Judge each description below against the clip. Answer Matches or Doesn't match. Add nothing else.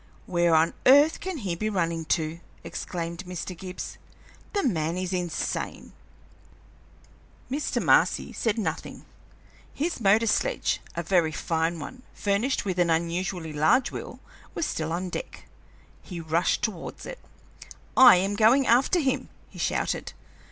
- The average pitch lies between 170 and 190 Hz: Matches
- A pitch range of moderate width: Doesn't match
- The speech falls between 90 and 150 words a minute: Matches